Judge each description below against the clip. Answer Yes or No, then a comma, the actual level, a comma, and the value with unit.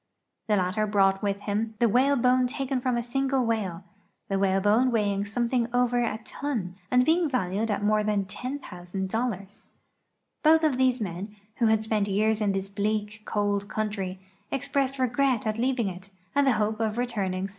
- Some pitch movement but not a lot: Yes, average, 3.9 semitones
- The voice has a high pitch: Yes, high, 220 Hz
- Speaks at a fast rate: No, average, 175 wpm